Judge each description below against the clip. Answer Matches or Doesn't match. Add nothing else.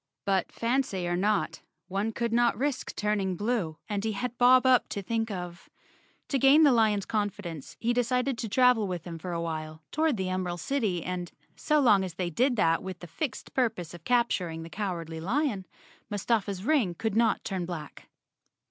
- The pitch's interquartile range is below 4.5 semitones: Doesn't match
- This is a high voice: Matches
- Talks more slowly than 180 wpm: Doesn't match